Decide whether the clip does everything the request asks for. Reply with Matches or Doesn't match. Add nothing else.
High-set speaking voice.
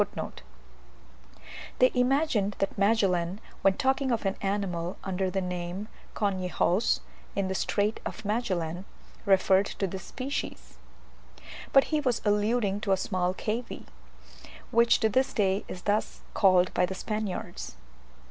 Matches